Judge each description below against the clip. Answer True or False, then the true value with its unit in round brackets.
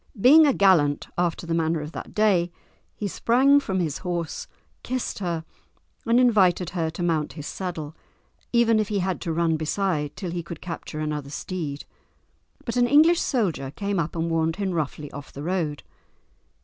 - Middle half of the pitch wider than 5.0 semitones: False (4.3 semitones)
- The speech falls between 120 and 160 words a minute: False (175 wpm)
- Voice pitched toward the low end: False (175 Hz)